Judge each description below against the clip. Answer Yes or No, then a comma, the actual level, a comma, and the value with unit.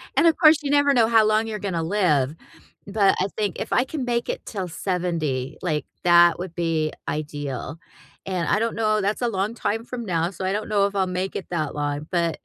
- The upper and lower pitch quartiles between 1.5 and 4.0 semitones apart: No, average, 4.8 semitones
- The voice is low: No, high, 190 Hz